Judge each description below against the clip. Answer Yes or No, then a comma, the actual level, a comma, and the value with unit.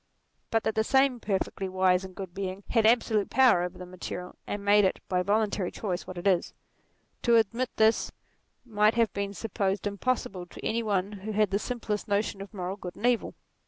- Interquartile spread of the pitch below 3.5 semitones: Yes, average, 2.8 semitones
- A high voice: Yes, high, 205 Hz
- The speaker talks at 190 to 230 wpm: Yes, average, 195 wpm